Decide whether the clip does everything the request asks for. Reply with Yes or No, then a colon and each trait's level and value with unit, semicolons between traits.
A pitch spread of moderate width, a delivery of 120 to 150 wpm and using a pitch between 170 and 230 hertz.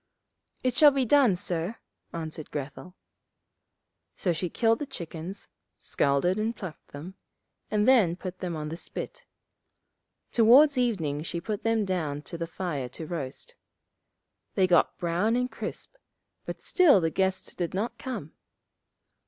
No: wide, 5.7 semitones; average, 145 wpm; medium, 185 Hz